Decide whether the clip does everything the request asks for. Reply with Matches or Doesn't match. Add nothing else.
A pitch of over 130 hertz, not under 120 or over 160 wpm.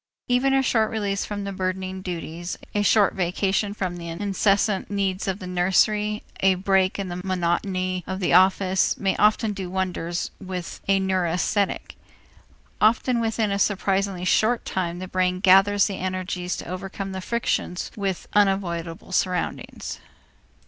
Matches